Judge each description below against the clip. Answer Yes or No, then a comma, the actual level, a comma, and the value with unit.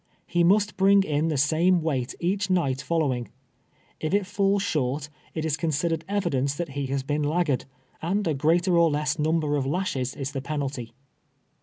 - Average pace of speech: Yes, average, 180 wpm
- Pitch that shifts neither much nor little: Yes, average, 4.0 semitones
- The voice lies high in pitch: No, medium, 155 Hz